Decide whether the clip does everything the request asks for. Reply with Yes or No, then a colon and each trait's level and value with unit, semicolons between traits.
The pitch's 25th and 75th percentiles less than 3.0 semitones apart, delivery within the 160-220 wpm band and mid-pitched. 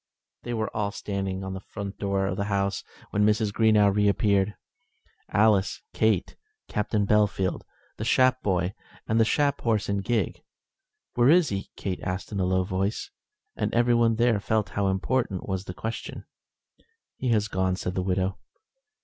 No: narrow, 2.5 semitones; average, 165 wpm; low, 100 Hz